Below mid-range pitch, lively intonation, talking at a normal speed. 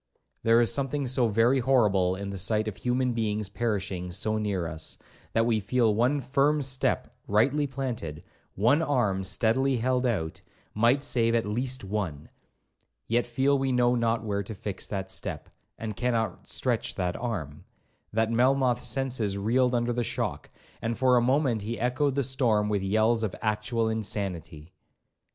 No: low, 115 Hz; average, 3.8 semitones; average, 160 wpm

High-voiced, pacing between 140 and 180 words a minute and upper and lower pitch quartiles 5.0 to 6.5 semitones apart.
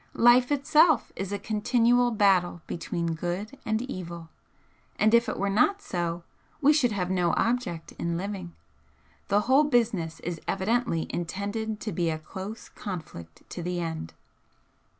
Yes: high, 200 Hz; average, 150 wpm; wide, 5.5 semitones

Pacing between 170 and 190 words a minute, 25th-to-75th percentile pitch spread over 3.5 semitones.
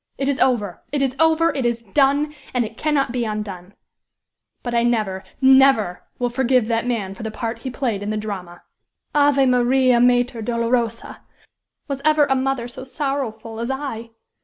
No: average, 175 wpm; average, 3.2 semitones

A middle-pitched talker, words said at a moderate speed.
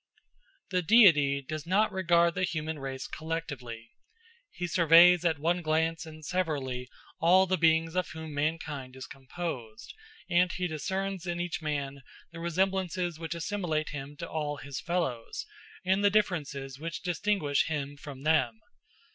Yes: medium, 160 Hz; average, 145 wpm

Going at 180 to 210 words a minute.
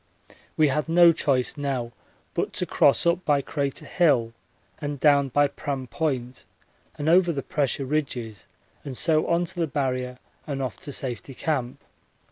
No: average, 160 wpm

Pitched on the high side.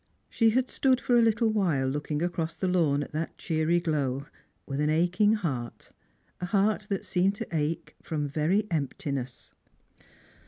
No: medium, 165 Hz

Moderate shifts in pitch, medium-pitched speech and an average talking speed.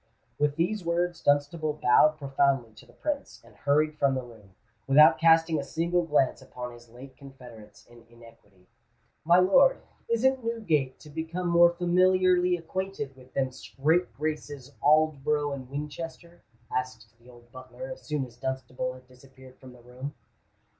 Yes: average, 4.9 semitones; medium, 145 Hz; average, 155 wpm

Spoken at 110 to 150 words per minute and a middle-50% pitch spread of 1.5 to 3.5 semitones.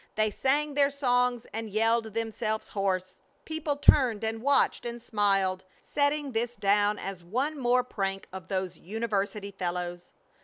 No: average, 145 wpm; average, 4.2 semitones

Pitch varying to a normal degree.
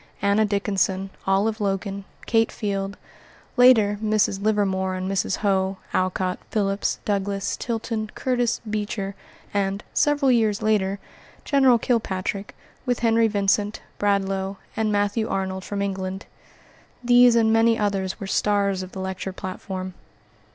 No: narrow, 2.3 semitones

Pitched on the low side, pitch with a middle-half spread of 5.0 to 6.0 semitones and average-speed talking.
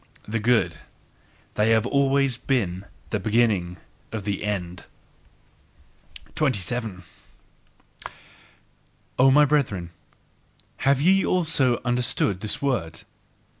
No: low, 115 Hz; wide, 5.4 semitones; slow, 95 wpm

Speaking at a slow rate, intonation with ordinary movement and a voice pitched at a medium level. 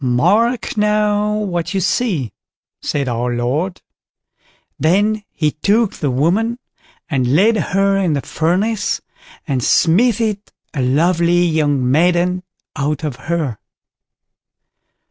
No: slow, 110 wpm; wide, 6.4 semitones; medium, 170 Hz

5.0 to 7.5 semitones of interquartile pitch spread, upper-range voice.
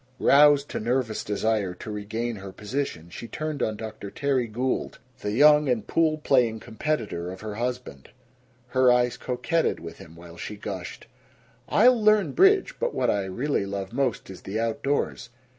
No: wide, 5.6 semitones; low, 115 Hz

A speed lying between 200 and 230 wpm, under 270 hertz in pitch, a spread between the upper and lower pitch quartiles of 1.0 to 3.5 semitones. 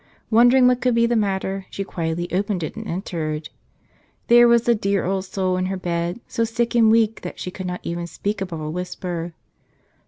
No: fast, 205 wpm; high, 190 Hz; average, 4.5 semitones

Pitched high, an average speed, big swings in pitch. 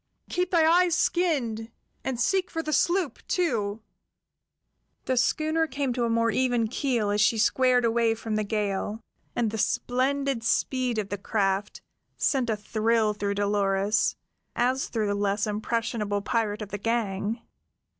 No: high, 230 Hz; average, 155 wpm; average, 3.8 semitones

